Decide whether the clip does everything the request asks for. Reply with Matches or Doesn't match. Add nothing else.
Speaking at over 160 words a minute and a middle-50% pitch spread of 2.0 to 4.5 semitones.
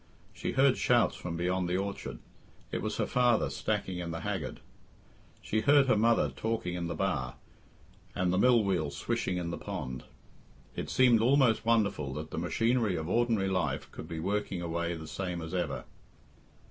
Doesn't match